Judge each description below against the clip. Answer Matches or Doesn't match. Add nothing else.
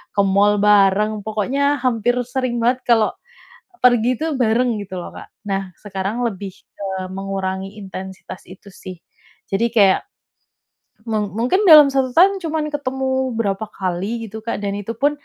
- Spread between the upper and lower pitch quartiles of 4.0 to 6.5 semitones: Matches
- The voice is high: Matches